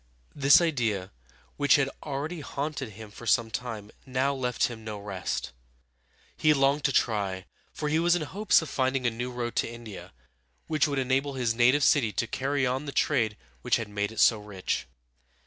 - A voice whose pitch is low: Yes, low, 125 Hz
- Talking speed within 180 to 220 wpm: Yes, average, 185 wpm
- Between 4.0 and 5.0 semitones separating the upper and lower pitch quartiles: Yes, average, 4.3 semitones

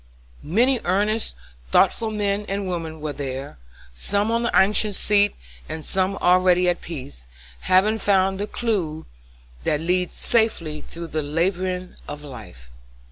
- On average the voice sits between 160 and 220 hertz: Yes, medium, 185 Hz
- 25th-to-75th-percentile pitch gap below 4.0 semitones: No, average, 4.7 semitones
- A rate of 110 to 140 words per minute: Yes, slow, 135 wpm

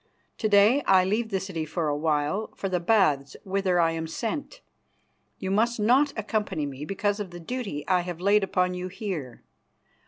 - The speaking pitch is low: No, high, 190 Hz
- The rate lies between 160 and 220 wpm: Yes, average, 185 wpm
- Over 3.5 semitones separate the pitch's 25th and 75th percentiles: Yes, average, 4.3 semitones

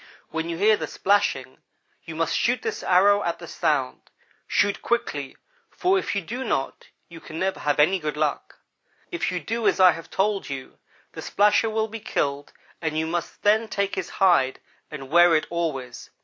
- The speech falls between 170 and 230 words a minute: Yes, average, 190 wpm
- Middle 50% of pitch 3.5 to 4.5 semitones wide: No, average, 5.1 semitones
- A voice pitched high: No, medium, 175 Hz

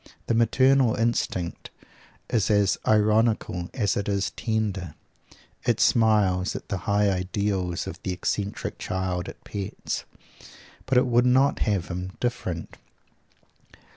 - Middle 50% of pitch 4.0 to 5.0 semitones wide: No, average, 3.6 semitones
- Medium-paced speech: No, slow, 125 wpm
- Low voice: Yes, low, 100 Hz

